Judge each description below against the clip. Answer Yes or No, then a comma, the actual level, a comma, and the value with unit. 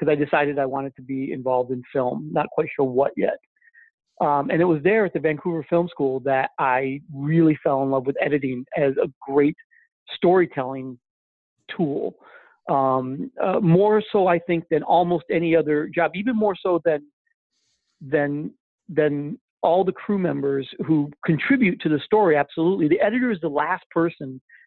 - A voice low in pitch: No, medium, 155 Hz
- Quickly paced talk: No, average, 175 wpm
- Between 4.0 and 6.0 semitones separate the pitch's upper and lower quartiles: Yes, average, 4.6 semitones